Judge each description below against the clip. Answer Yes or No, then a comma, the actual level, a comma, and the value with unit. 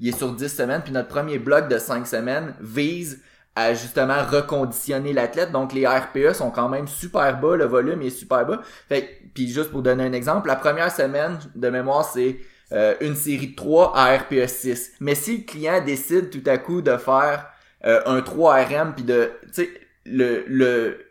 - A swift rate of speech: No, average, 195 wpm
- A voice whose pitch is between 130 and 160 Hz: Yes, medium, 140 Hz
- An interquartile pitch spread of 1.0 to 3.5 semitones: Yes, average, 2.8 semitones